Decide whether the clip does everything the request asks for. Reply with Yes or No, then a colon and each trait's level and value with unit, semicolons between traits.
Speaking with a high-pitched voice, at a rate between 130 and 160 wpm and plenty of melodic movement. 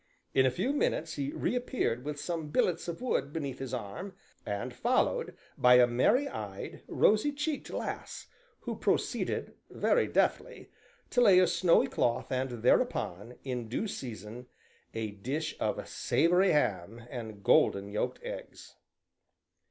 No: low, 135 Hz; average, 140 wpm; wide, 7.9 semitones